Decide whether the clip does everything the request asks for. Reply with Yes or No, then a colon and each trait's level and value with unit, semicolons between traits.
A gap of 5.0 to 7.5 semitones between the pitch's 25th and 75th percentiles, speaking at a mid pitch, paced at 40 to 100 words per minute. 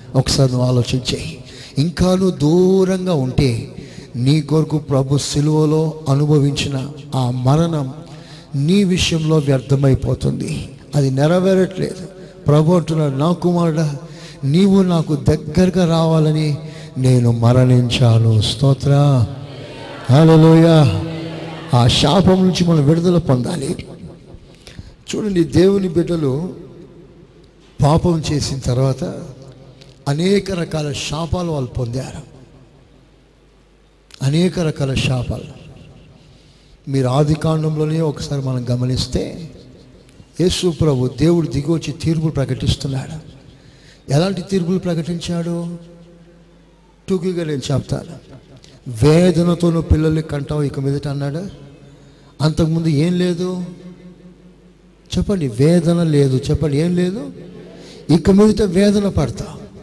No: average, 4.0 semitones; medium, 155 Hz; average, 85 wpm